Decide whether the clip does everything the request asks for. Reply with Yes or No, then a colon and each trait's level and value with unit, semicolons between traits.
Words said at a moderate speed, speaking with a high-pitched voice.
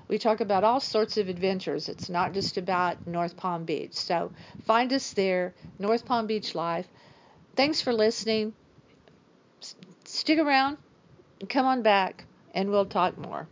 Yes: average, 160 wpm; high, 210 Hz